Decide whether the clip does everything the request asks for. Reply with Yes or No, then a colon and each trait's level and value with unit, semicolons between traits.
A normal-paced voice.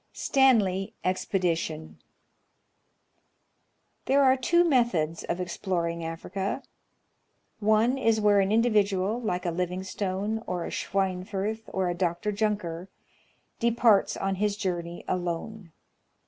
No: slow, 105 wpm